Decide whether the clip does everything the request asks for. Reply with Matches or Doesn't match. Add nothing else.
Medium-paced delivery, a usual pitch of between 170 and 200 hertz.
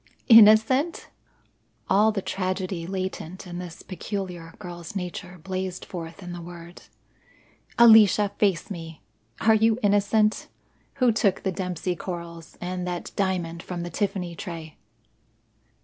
Doesn't match